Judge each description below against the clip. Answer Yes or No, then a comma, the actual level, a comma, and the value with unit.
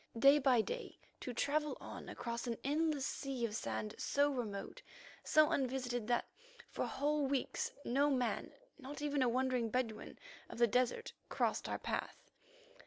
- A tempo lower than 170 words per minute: Yes, average, 155 wpm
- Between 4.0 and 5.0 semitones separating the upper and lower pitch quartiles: No, average, 3.3 semitones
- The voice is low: No, very high, 260 Hz